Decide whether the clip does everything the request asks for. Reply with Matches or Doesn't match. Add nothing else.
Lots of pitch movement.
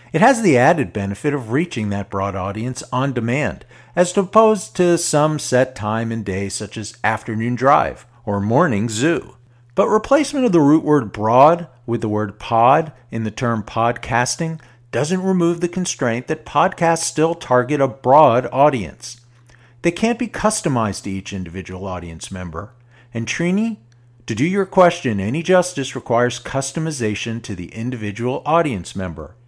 Matches